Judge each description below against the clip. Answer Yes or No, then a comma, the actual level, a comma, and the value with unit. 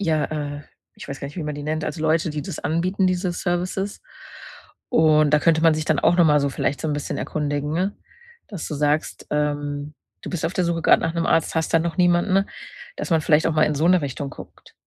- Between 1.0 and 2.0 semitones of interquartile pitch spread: No, narrow, 2.6 semitones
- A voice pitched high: No, medium, 155 Hz